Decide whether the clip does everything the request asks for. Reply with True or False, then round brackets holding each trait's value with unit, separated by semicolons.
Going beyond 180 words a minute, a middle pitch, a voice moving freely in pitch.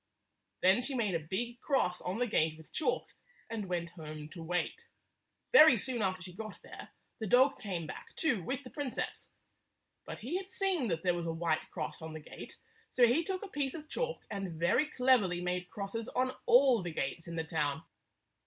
False (205 wpm; 200 Hz; 7.4 semitones)